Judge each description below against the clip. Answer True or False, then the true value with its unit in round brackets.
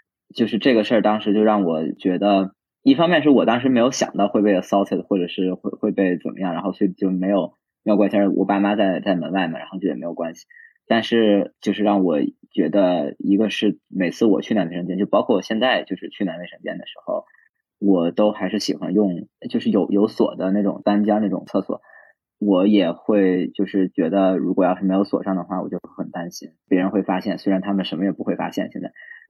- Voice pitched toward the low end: True (100 Hz)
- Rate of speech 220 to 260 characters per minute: False (330 characters per minute)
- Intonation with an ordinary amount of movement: False (1.9 semitones)